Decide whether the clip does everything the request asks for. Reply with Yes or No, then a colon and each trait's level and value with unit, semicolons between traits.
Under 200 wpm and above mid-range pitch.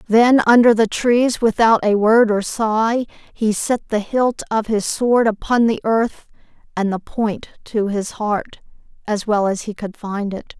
Yes: average, 175 wpm; high, 220 Hz